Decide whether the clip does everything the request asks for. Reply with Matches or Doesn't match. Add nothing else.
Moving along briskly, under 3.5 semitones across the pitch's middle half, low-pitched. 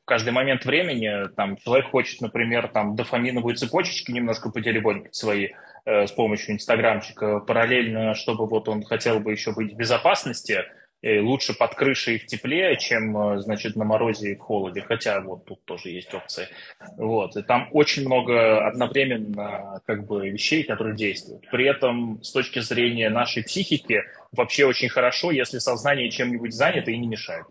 Matches